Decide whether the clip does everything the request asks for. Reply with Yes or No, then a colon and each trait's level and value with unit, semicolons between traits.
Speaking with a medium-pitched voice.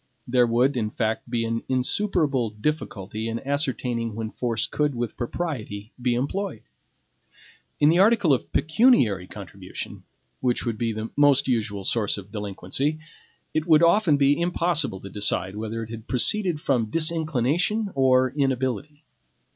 No: low, 130 Hz